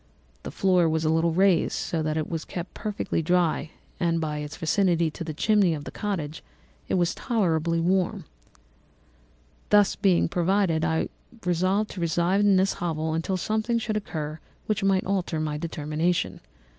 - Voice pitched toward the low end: No, medium, 170 Hz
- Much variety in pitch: No, average, 3.2 semitones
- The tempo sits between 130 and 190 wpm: Yes, average, 165 wpm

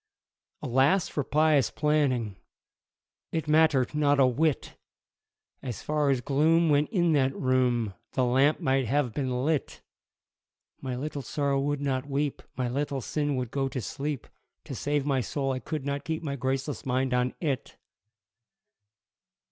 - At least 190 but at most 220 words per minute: No, average, 150 wpm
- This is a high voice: No, medium, 140 Hz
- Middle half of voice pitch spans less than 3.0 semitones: Yes, narrow, 2.4 semitones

